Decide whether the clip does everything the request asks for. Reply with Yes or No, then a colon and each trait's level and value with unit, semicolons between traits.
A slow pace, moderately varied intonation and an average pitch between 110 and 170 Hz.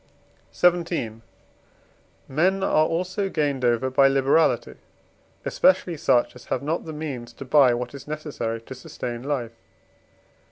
Yes: slow, 130 wpm; average, 4.7 semitones; medium, 140 Hz